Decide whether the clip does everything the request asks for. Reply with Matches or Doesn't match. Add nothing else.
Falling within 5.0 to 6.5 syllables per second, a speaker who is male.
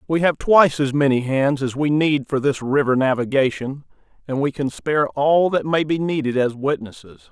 Matches